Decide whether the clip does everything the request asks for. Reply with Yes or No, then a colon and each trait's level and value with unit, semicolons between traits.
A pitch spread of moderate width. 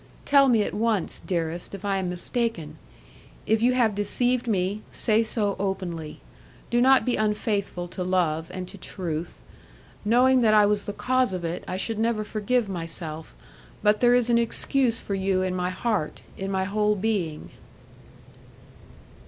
Yes: average, 4.0 semitones